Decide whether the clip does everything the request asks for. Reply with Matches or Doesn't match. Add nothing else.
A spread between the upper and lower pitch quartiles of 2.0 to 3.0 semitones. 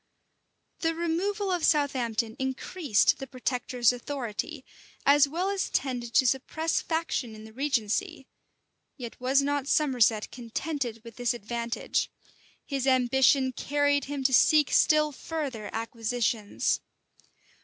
Doesn't match